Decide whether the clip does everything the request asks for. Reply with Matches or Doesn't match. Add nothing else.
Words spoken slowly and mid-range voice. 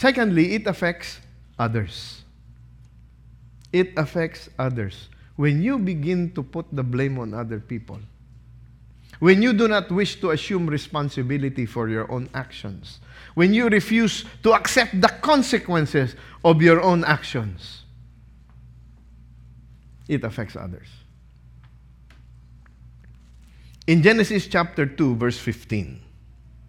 Doesn't match